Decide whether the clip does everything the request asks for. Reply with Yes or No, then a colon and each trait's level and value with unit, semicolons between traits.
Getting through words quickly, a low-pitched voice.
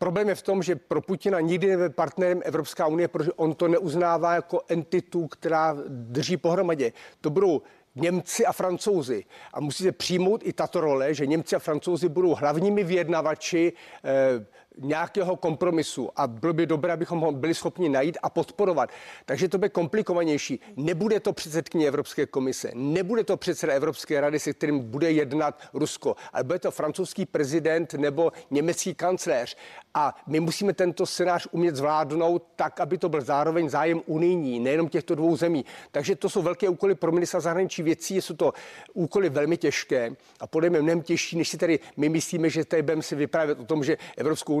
No: fast, 175 wpm; medium, 170 Hz